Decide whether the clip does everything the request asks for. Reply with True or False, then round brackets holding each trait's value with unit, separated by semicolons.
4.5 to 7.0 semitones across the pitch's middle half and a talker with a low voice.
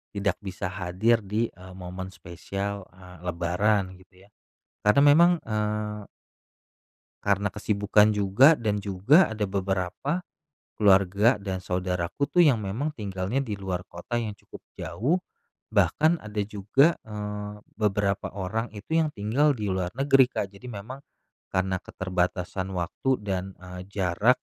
False (3.3 semitones; 100 Hz)